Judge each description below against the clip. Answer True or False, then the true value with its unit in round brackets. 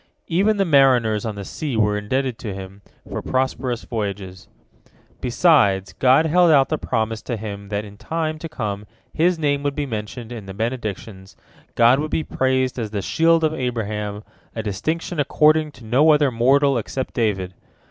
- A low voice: True (125 Hz)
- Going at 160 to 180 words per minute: True (175 wpm)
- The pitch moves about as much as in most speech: False (5.9 semitones)